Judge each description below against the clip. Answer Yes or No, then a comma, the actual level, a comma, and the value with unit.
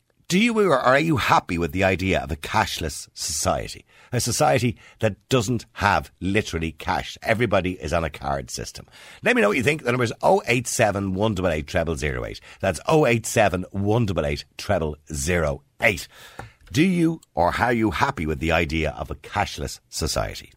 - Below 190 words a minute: Yes, average, 155 wpm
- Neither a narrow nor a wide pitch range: No, wide, 7.0 semitones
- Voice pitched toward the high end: No, low, 100 Hz